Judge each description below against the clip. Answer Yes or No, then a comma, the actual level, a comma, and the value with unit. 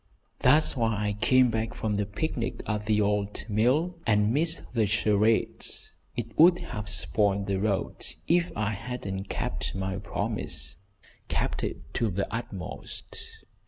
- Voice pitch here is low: Yes, low, 105 Hz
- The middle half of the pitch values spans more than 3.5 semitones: No, average, 3.0 semitones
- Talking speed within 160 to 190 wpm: No, average, 145 wpm